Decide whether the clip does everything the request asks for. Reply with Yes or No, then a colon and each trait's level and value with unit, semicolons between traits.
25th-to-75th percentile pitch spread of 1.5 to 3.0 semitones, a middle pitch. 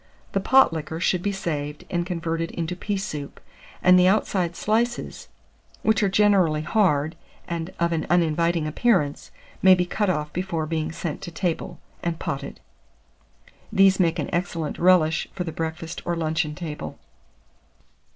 Yes: average, 2.7 semitones; medium, 170 Hz